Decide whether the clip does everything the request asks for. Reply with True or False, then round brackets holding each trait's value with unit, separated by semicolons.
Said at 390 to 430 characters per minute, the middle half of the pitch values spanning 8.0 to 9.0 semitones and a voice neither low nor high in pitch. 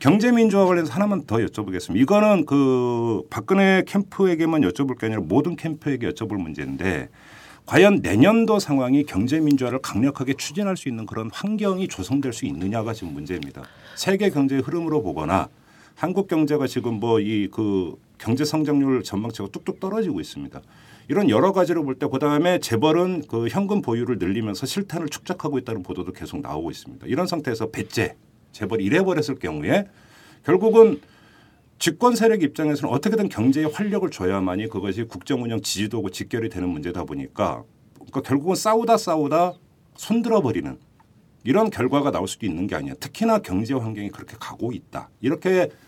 True (395 characters per minute; 8.4 semitones; 145 Hz)